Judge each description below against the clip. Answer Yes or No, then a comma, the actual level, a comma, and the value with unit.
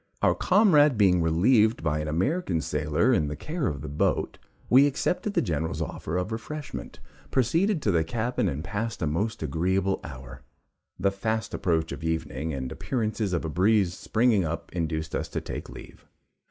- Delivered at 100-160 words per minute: No, average, 175 wpm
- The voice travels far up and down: Yes, wide, 6.5 semitones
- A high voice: No, very low, 95 Hz